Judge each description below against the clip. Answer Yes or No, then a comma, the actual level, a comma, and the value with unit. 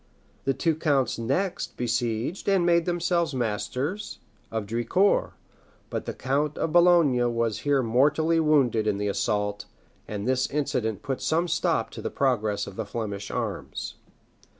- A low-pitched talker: Yes, low, 130 Hz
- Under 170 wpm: Yes, average, 150 wpm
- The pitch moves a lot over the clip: Yes, wide, 6.3 semitones